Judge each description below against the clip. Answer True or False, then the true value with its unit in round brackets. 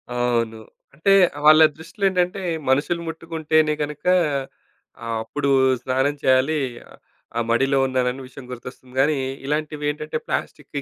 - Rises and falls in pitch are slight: False (3.3 semitones)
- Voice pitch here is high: False (145 Hz)